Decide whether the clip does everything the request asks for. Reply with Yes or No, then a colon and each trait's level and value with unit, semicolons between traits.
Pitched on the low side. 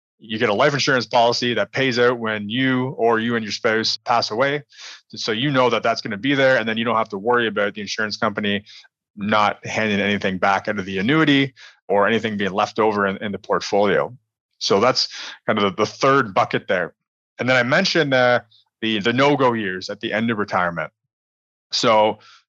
Yes: low, 110 Hz